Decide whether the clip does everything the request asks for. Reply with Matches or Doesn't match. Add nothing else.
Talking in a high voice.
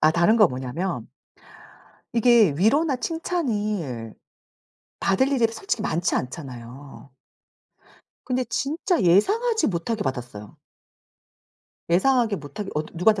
Matches